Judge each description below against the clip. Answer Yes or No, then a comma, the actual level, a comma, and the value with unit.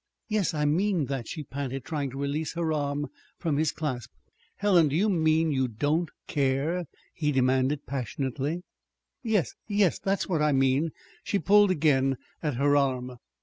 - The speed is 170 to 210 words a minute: No, average, 160 wpm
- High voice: No, medium, 150 Hz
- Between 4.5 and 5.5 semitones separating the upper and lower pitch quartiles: No, average, 3.8 semitones